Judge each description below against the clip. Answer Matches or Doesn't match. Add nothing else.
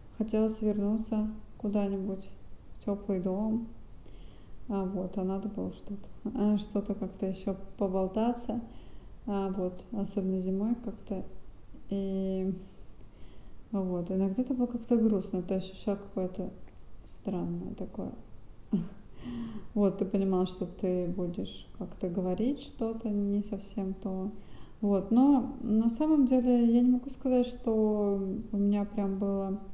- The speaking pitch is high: Matches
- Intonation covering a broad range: Doesn't match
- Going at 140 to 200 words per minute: Doesn't match